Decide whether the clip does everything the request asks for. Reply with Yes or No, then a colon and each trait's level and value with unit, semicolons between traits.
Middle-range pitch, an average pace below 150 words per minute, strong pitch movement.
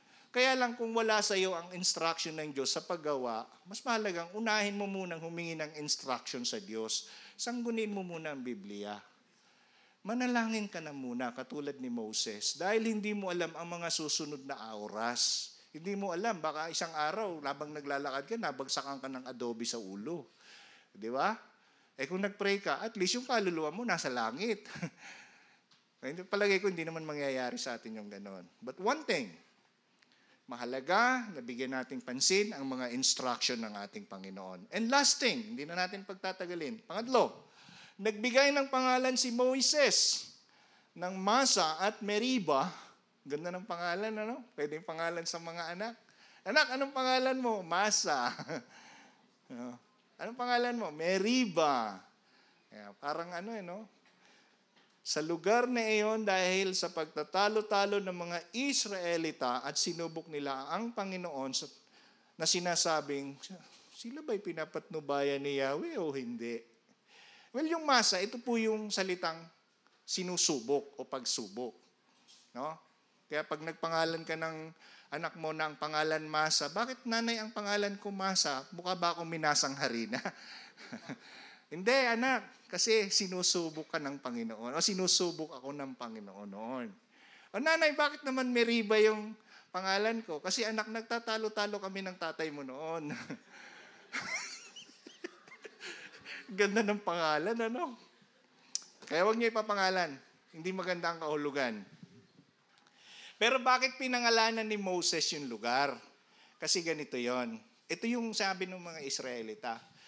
Yes: medium, 180 Hz; average, 135 wpm; wide, 6.7 semitones